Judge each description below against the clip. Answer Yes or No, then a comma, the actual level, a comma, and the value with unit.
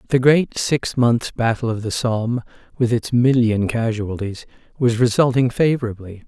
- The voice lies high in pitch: No, low, 120 Hz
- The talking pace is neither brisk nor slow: Yes, average, 145 wpm